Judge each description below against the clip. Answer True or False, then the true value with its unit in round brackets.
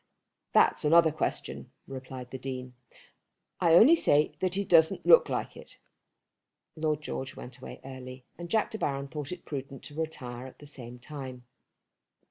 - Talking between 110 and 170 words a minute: True (160 wpm)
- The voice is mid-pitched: True (145 Hz)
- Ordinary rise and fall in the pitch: True (3.9 semitones)